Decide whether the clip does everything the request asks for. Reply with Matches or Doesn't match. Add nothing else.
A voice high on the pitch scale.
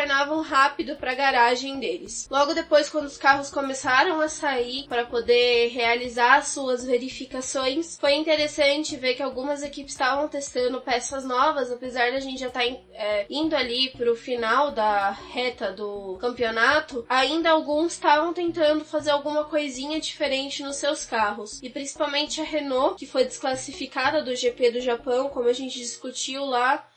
Matches